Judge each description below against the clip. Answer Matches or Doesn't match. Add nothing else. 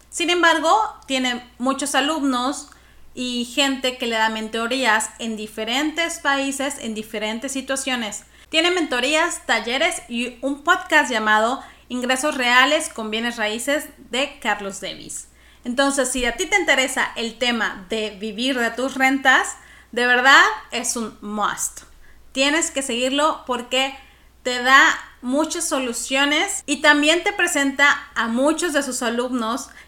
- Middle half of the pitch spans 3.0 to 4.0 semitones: Matches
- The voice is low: Doesn't match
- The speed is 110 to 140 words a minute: Matches